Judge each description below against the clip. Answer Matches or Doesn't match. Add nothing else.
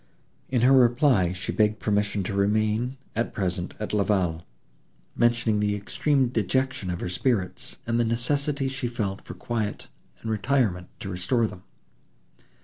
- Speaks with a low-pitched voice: Matches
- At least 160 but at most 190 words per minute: Doesn't match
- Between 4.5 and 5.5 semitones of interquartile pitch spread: Doesn't match